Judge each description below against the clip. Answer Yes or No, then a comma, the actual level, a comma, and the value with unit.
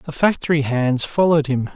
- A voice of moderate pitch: Yes, medium, 145 Hz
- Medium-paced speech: Yes, average, 170 wpm